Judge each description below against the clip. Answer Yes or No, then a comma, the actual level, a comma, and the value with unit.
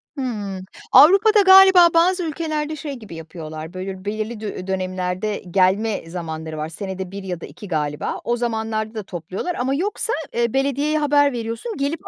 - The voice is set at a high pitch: Yes, high, 220 Hz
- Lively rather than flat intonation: Yes, wide, 7.9 semitones